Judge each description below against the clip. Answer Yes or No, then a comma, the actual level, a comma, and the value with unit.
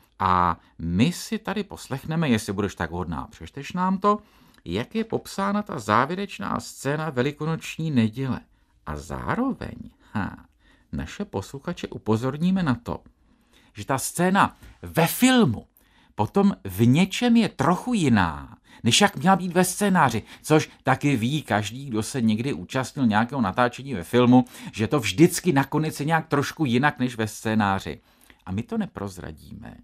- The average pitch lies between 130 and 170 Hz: Yes, low, 135 Hz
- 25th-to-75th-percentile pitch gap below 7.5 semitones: No, wide, 8.4 semitones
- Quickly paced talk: No, average, 145 wpm